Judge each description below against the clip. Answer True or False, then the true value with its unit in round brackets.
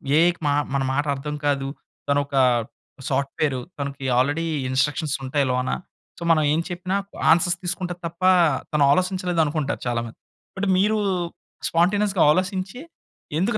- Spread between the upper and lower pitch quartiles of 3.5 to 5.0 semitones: True (4.5 semitones)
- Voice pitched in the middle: True (160 Hz)